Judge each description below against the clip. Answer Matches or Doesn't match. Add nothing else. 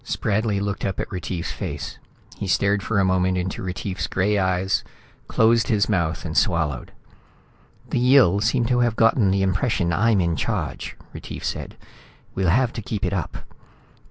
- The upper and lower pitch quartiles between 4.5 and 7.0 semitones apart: Doesn't match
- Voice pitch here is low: Matches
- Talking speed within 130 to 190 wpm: Matches